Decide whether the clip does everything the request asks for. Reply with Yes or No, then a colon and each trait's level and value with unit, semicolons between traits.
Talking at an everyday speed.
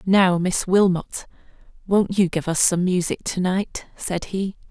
Yes: average, 165 wpm